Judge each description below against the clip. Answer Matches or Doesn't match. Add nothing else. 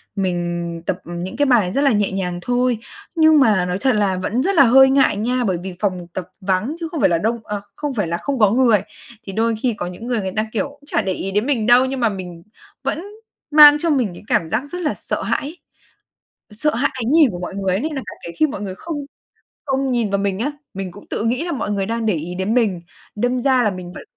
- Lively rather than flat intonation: Matches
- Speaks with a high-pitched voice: Matches